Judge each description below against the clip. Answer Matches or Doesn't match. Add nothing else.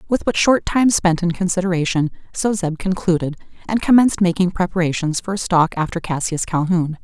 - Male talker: Doesn't match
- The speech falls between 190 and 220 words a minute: Doesn't match